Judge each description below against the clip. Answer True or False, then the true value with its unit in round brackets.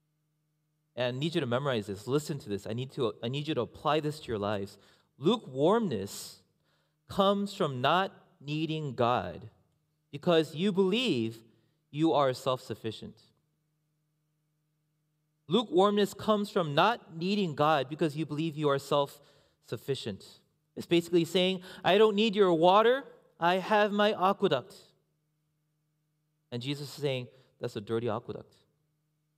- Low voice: False (150 Hz)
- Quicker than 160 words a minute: False (140 wpm)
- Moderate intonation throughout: True (4.1 semitones)